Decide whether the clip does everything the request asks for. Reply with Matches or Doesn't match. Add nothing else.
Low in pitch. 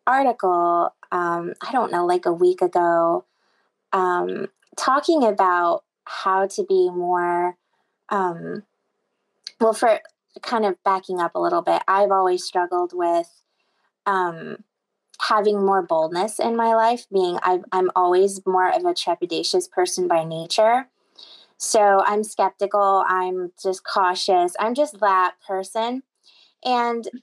Doesn't match